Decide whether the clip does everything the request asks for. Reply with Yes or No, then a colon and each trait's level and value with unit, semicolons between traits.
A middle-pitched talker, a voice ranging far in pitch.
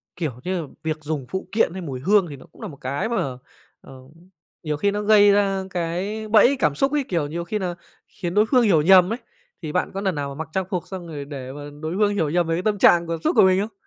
No: medium, 180 Hz; average, 4.8 semitones